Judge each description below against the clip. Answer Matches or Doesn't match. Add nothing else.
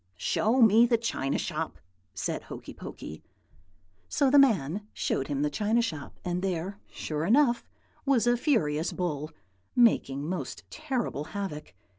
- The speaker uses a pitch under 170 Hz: Doesn't match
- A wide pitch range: Matches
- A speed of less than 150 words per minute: Matches